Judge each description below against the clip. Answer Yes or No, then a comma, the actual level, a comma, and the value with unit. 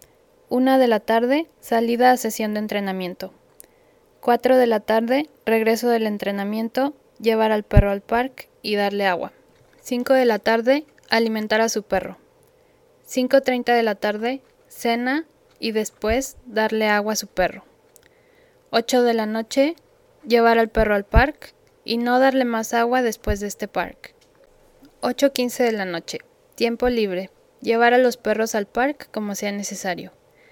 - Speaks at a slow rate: No, average, 150 wpm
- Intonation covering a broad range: No, average, 3.9 semitones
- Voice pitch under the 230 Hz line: No, high, 235 Hz